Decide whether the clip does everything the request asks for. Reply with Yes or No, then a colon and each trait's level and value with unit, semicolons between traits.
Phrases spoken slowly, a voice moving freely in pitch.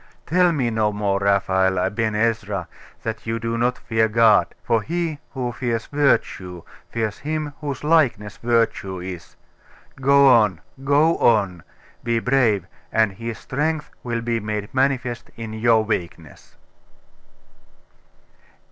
No: slow, 130 wpm; average, 4.1 semitones